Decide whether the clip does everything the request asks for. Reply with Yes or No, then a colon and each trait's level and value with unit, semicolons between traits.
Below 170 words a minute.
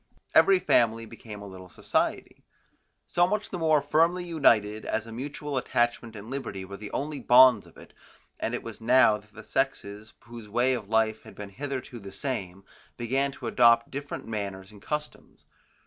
No: average, 180 wpm